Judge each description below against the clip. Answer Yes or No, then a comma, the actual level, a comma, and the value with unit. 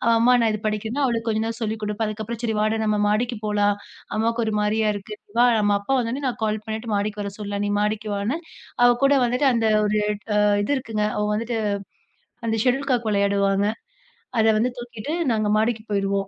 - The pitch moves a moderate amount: No, narrow, 2.0 semitones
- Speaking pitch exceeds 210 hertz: Yes, high, 220 Hz